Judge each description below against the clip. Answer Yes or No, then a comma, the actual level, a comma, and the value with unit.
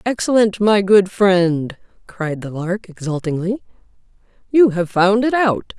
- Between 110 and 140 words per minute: Yes, slow, 135 wpm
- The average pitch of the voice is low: No, high, 195 Hz